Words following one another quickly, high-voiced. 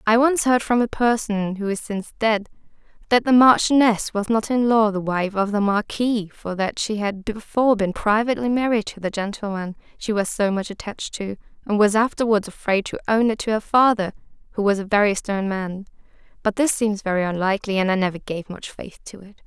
Yes: fast, 210 wpm; high, 210 Hz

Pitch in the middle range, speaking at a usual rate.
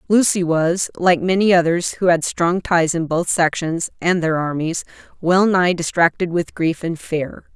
Yes: medium, 170 Hz; average, 175 wpm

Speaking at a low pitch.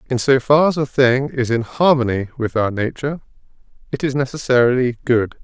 Yes: low, 130 Hz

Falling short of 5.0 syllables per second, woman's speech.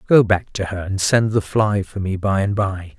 No: 4.6 syllables/s; male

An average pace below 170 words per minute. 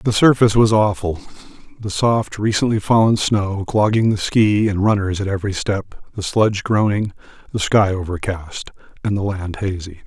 Yes: average, 160 wpm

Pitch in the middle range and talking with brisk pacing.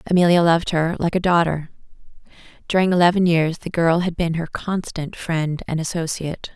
No: medium, 170 Hz; average, 165 wpm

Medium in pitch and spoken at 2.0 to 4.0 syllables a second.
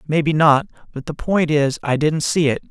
No: medium, 150 Hz; 5.0 syllables/s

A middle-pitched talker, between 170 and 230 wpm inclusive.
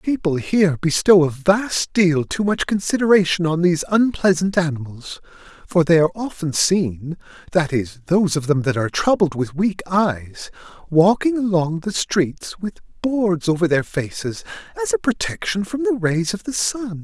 No: medium, 175 Hz; average, 160 wpm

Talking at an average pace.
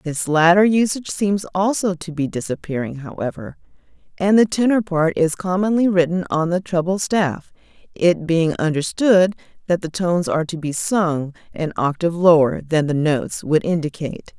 Yes: average, 160 wpm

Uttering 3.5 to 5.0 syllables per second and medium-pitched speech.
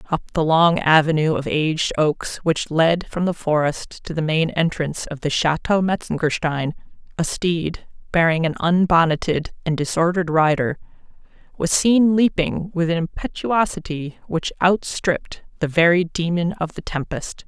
Yes: 4.6 syllables/s; medium, 165 Hz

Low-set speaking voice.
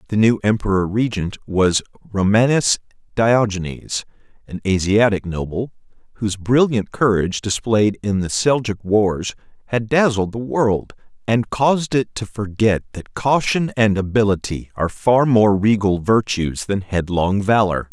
Yes: low, 105 Hz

